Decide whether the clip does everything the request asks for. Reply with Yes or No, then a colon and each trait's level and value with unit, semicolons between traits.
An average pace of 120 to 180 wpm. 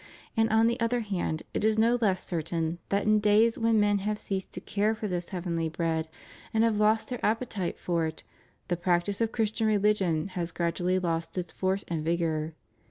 No: average, 200 wpm